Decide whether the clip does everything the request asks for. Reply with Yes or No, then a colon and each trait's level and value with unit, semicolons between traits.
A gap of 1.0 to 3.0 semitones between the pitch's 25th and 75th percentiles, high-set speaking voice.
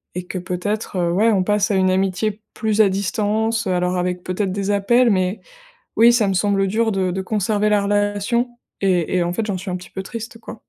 Yes: average, 2.7 semitones; high, 200 Hz